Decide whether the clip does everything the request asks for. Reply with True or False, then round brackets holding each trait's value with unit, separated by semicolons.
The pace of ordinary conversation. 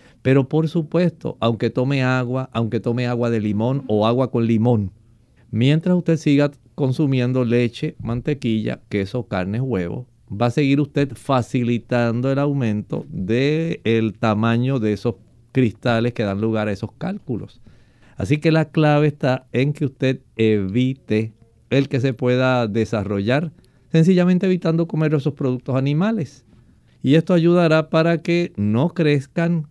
True (140 wpm)